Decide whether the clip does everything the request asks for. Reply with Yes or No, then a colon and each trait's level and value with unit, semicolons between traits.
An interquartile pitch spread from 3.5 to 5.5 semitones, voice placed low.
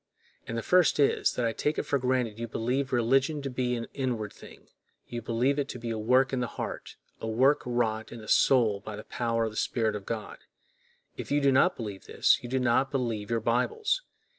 No: average, 3.0 semitones; low, 120 Hz